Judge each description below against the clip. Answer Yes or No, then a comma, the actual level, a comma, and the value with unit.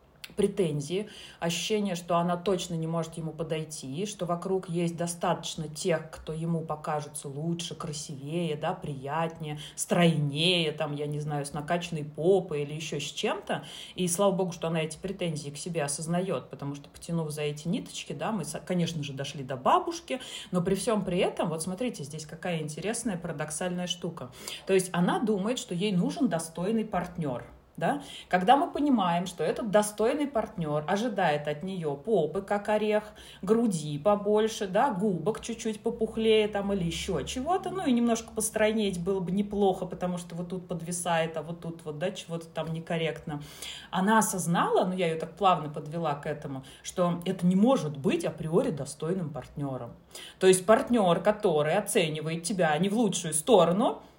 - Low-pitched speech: No, medium, 175 Hz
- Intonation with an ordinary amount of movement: Yes, average, 4.5 semitones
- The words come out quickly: Yes, fast, 165 wpm